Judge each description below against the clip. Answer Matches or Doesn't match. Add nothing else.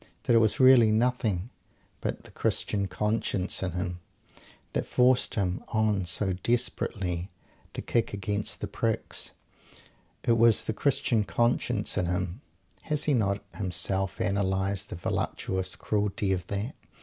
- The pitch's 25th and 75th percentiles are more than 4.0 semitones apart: Doesn't match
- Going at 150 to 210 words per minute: Doesn't match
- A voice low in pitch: Matches